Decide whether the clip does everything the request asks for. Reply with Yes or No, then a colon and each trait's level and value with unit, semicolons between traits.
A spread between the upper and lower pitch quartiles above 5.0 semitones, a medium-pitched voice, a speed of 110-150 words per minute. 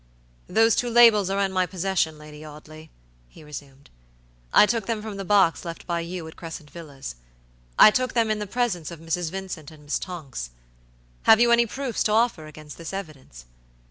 No: wide, 5.5 semitones; medium, 175 Hz; average, 190 wpm